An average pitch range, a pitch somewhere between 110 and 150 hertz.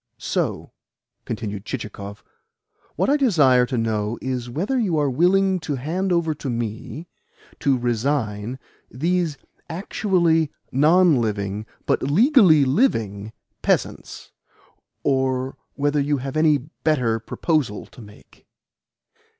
No: wide, 6.1 semitones; medium, 140 Hz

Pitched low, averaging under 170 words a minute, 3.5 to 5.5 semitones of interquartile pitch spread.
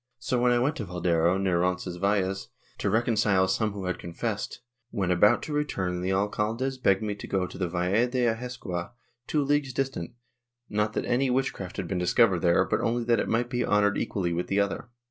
No: low, 100 Hz; fast, 205 wpm; average, 4.8 semitones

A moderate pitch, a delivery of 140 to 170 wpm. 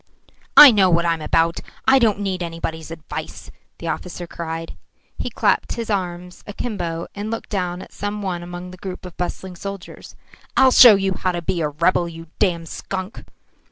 No: medium, 180 Hz; average, 185 wpm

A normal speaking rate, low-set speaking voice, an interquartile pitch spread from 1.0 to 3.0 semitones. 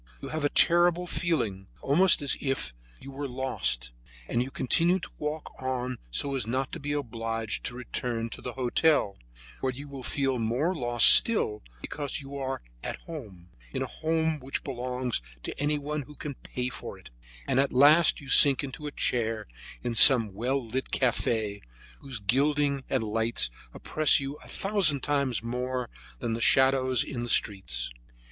No: average, 170 wpm; low, 130 Hz; average, 3.6 semitones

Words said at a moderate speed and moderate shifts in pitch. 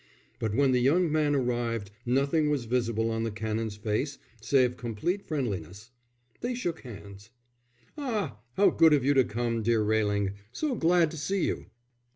No: average, 165 wpm; wide, 5.8 semitones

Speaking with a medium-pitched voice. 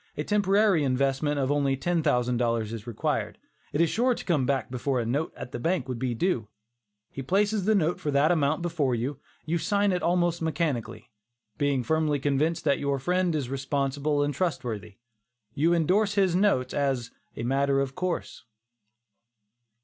Yes: medium, 145 Hz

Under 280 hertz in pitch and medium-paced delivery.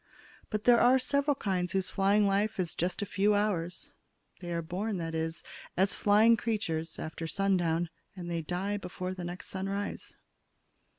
Yes: high, 190 Hz; average, 165 wpm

